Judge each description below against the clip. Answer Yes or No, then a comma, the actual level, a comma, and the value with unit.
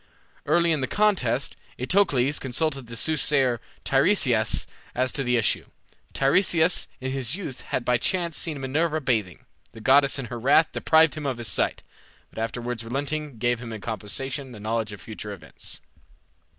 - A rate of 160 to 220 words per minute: Yes, average, 165 wpm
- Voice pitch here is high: No, low, 130 Hz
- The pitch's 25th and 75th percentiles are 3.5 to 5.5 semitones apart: Yes, average, 4.6 semitones